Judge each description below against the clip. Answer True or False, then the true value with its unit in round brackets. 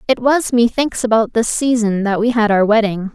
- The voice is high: True (225 Hz)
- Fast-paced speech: True (210 wpm)